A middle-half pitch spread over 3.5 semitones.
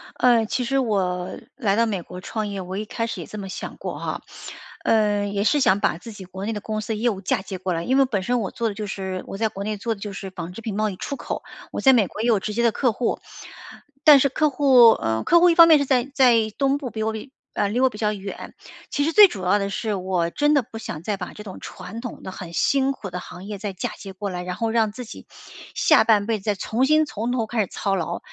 Yes: average, 3.9 semitones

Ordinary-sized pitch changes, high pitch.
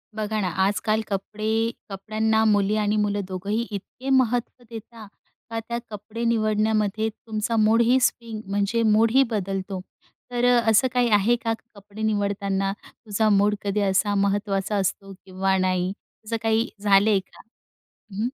No: narrow, 2.1 semitones; high, 215 Hz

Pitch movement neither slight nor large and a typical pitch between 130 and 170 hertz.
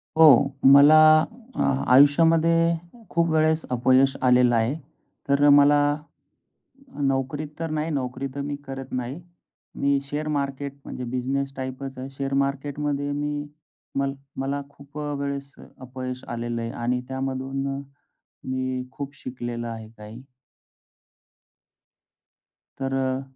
No: narrow, 1.9 semitones; low, 135 Hz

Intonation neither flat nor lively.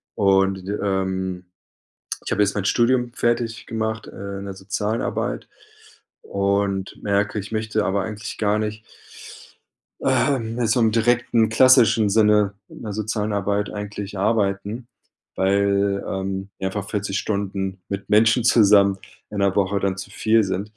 No: narrow, 2.0 semitones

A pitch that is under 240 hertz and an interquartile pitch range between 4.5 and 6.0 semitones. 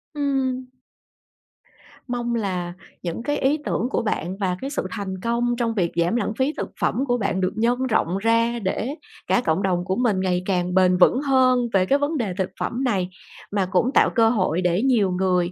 Yes: high, 215 Hz; average, 5.0 semitones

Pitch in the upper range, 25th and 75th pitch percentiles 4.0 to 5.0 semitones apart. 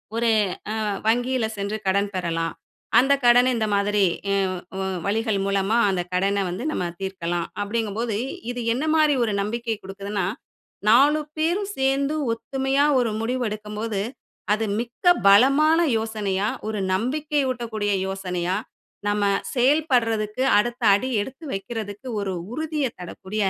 Yes: high, 220 Hz; average, 4.4 semitones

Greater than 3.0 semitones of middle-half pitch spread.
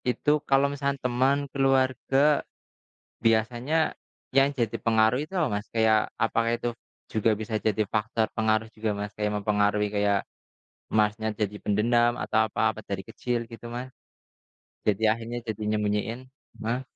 No: narrow, 2.6 semitones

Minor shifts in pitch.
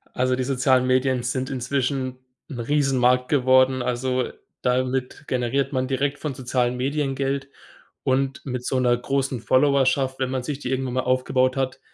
Yes: narrow, 1.2 semitones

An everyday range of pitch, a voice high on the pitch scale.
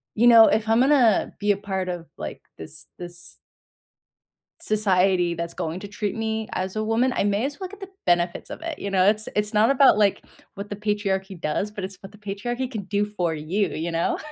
Yes: average, 3.2 semitones; high, 205 Hz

